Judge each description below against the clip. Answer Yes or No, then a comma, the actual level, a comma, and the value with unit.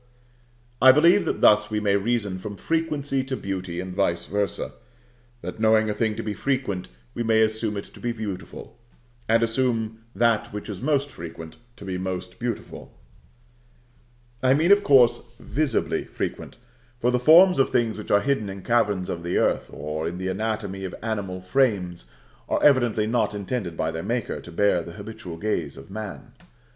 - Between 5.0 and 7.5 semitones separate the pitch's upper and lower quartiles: No, average, 4.5 semitones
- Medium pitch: No, low, 110 Hz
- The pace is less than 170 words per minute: No, average, 175 wpm